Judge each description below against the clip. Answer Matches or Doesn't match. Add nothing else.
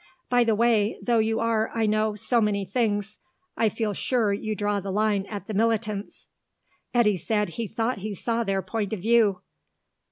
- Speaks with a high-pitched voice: Matches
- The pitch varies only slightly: Matches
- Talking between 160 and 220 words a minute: Matches